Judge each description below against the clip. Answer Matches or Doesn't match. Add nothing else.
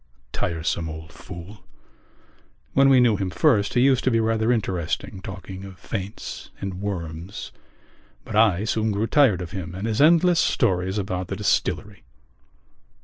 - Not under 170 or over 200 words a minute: Doesn't match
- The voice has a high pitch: Doesn't match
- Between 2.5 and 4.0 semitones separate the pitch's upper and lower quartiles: Matches